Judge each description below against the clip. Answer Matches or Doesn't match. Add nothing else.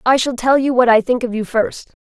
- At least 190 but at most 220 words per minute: Doesn't match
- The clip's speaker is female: Matches